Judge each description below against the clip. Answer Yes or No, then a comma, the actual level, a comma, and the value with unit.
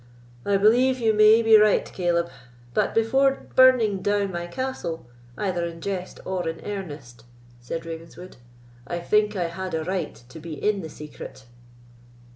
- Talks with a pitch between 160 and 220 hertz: Yes, high, 190 Hz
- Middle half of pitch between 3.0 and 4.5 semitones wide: Yes, average, 4.2 semitones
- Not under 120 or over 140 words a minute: No, average, 155 wpm